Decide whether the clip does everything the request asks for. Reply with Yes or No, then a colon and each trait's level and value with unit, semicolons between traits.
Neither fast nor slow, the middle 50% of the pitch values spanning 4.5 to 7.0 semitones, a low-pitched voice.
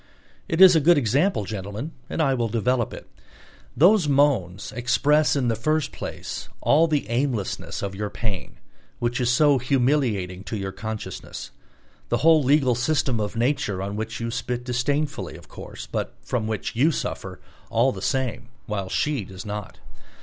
Yes: average, 165 wpm; average, 5.3 semitones; low, 125 Hz